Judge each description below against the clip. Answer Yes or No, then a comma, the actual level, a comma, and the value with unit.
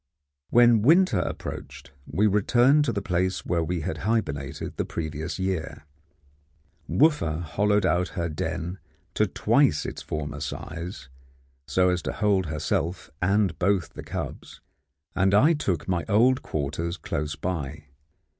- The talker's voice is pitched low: Yes, very low, 90 Hz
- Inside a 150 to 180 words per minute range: No, slow, 135 wpm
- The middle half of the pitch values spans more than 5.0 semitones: No, average, 4.7 semitones